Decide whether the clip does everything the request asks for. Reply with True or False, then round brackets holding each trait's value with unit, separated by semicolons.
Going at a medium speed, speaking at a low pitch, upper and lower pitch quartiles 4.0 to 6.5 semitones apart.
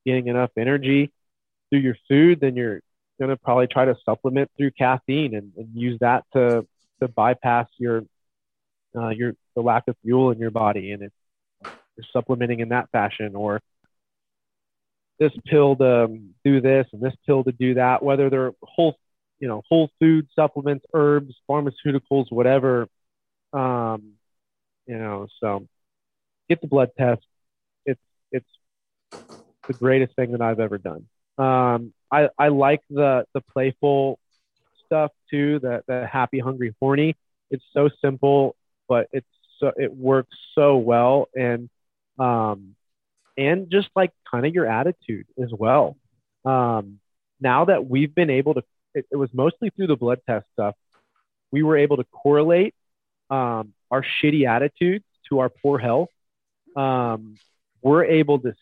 False (155 wpm; 130 Hz; 3.3 semitones)